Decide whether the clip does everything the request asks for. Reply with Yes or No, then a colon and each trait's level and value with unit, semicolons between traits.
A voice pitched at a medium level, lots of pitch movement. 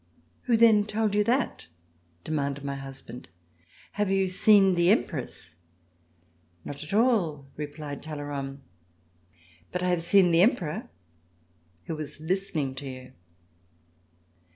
Yes: medium, 160 Hz; wide, 6.1 semitones